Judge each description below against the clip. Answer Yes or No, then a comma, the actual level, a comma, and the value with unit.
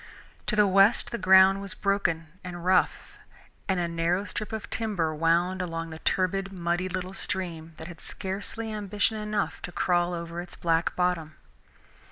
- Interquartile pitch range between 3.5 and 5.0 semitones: No, narrow, 2.6 semitones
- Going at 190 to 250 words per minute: No, average, 165 wpm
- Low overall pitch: No, medium, 185 Hz